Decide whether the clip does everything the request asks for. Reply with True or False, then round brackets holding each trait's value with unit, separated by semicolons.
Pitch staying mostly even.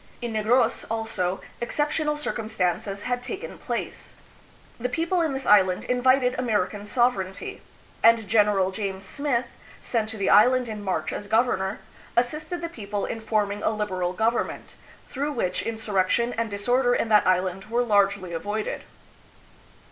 False (3.7 semitones)